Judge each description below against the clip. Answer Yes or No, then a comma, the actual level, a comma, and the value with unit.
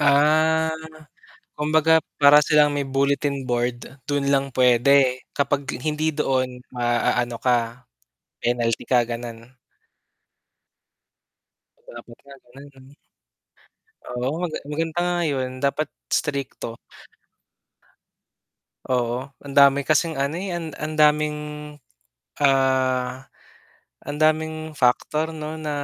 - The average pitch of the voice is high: No, medium, 140 Hz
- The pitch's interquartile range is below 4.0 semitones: Yes, average, 3.3 semitones